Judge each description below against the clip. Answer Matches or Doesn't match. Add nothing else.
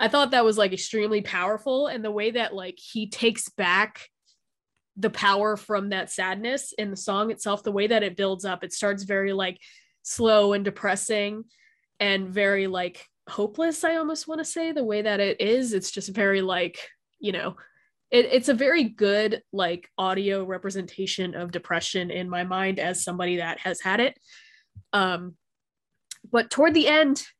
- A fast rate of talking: Doesn't match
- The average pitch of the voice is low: Doesn't match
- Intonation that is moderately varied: Matches